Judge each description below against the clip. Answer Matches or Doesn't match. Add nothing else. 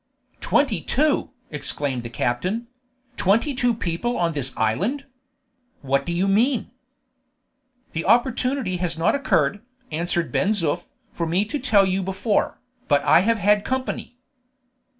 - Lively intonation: Matches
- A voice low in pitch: Doesn't match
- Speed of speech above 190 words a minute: Doesn't match